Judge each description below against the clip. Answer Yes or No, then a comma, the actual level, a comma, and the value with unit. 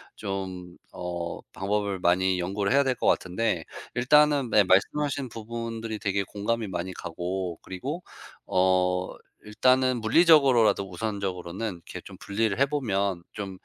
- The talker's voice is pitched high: No, low, 100 Hz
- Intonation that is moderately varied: Yes, average, 4.0 semitones